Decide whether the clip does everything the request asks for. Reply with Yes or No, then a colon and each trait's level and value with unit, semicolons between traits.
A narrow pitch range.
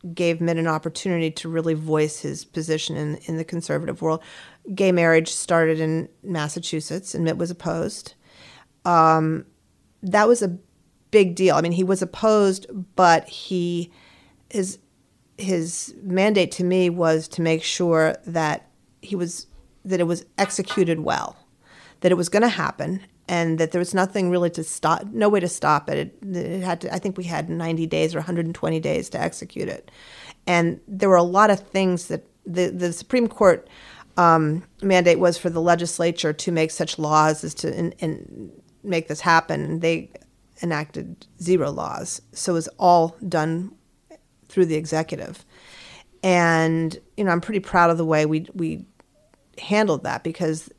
Yes: narrow, 2.3 semitones